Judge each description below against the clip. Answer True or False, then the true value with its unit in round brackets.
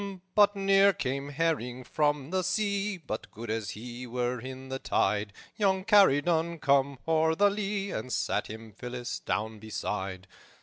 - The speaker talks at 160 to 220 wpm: False (150 wpm)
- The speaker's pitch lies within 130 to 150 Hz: True (140 Hz)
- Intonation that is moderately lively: False (8.0 semitones)